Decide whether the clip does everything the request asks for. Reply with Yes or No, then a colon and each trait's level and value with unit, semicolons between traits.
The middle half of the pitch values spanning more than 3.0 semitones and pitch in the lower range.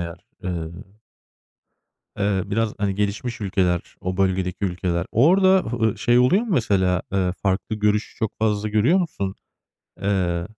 Yes: average, 3.4 semitones; low, 100 Hz